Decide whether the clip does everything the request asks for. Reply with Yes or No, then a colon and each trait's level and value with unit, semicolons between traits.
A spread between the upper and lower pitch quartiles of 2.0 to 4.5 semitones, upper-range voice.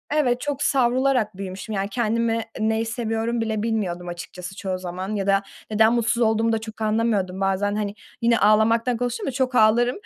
Yes: average, 2.9 semitones; high, 220 Hz